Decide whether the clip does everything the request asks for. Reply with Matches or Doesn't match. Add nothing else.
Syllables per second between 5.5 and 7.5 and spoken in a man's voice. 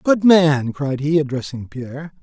Doesn't match